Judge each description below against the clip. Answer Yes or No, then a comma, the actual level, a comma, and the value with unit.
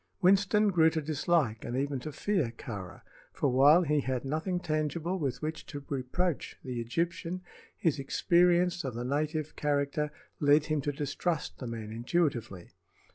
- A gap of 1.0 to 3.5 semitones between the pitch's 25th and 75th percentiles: No, average, 4.4 semitones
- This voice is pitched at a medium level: Yes, medium, 150 Hz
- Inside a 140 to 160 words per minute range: Yes, average, 155 wpm